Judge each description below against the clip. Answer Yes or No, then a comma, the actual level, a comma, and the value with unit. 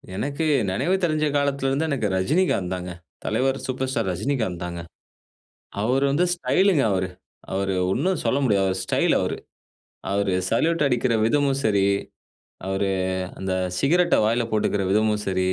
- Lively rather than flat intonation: Yes, wide, 6.6 semitones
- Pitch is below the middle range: Yes, low, 120 Hz